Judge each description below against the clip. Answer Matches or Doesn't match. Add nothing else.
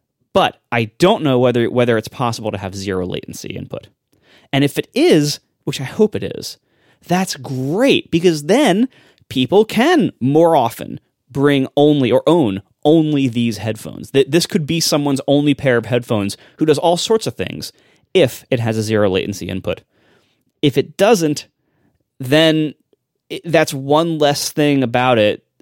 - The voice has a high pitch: Doesn't match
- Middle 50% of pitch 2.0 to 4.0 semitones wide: Doesn't match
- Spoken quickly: Doesn't match